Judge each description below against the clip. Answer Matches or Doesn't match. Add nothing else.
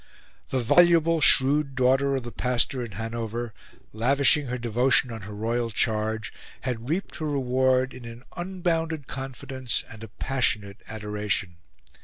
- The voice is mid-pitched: Doesn't match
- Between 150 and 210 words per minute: Doesn't match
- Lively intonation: Doesn't match